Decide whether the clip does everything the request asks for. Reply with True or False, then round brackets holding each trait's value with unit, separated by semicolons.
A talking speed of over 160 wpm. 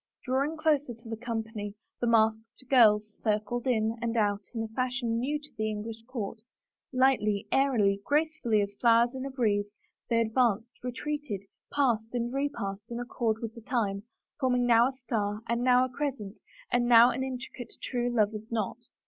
True (175 wpm)